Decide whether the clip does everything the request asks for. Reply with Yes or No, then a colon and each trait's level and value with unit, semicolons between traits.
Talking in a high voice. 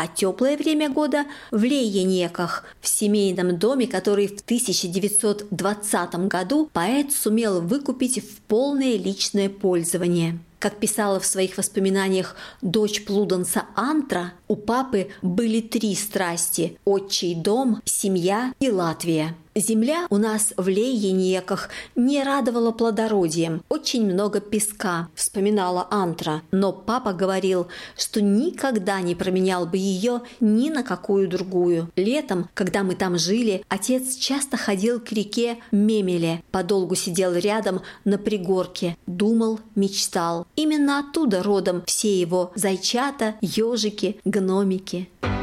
Yes: high, 200 Hz